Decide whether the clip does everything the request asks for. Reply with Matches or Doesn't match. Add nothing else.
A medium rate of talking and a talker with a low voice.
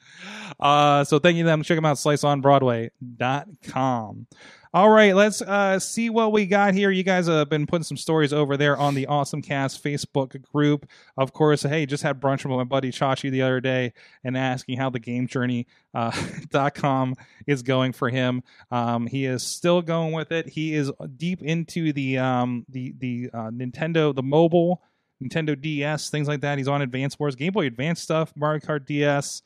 Doesn't match